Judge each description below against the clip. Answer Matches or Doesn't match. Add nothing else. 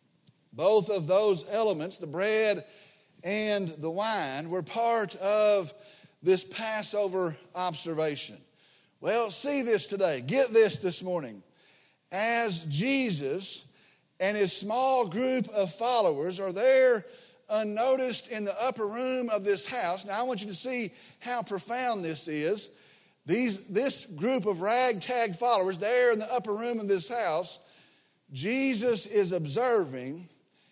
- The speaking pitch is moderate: Doesn't match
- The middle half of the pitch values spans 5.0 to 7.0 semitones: Doesn't match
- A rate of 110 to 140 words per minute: Matches